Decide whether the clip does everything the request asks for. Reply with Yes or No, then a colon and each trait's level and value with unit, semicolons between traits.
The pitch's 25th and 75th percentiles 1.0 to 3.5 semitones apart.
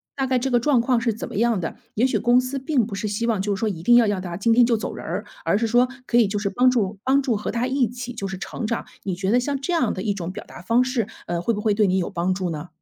No: average, 4.0 semitones